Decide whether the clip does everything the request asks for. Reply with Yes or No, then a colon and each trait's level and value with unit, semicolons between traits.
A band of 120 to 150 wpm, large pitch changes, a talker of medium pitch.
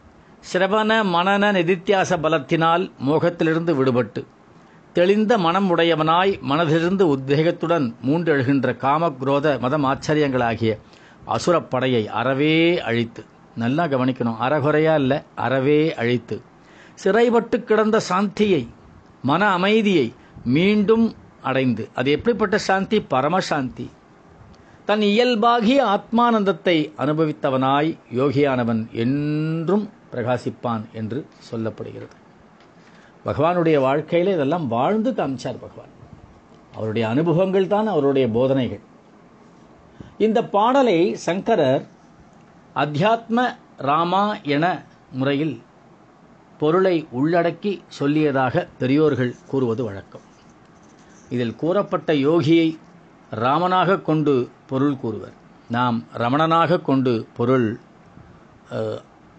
No: average, 80 wpm; wide, 6.2 semitones; medium, 155 Hz